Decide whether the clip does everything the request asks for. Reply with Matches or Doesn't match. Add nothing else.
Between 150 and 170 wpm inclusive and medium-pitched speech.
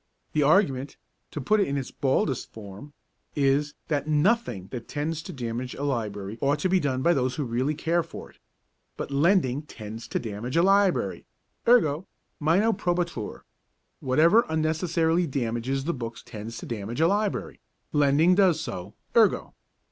Matches